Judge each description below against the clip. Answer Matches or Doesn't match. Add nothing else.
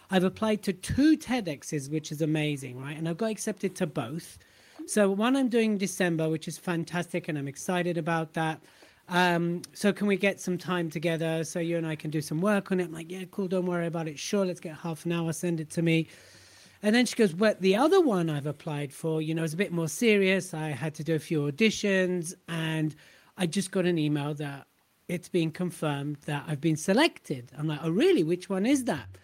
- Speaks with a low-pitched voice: Doesn't match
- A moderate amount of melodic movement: Matches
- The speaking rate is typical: Doesn't match